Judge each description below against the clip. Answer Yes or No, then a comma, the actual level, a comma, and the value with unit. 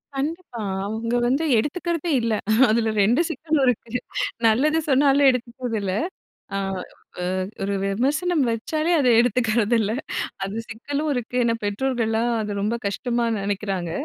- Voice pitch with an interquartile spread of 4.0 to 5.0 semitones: Yes, average, 4.4 semitones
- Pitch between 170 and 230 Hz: No, high, 240 Hz